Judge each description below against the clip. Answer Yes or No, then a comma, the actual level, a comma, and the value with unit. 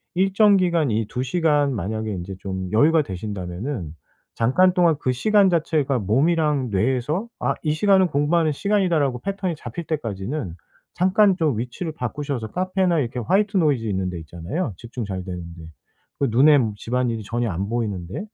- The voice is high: No, low, 135 Hz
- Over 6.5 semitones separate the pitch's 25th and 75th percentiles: Yes, wide, 7.9 semitones